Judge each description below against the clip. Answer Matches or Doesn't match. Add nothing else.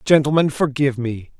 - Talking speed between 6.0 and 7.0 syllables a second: Doesn't match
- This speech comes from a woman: Doesn't match